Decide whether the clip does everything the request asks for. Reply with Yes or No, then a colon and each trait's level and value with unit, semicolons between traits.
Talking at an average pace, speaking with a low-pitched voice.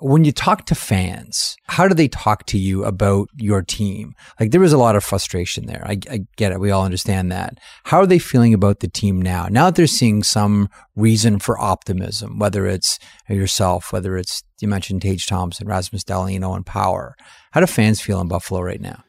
No: fast, 210 wpm; low, 105 Hz